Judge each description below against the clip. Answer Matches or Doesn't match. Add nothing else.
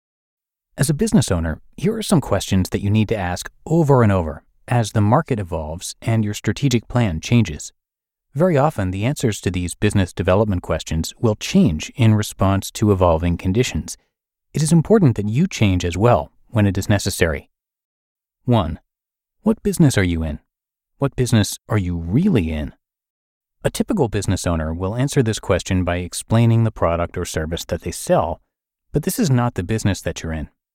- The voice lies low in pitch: Matches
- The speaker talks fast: Doesn't match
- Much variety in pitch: Matches